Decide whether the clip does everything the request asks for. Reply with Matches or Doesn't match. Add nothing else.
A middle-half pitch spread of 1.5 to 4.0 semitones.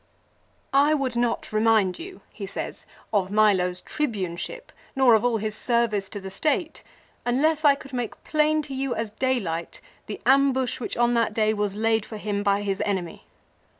Doesn't match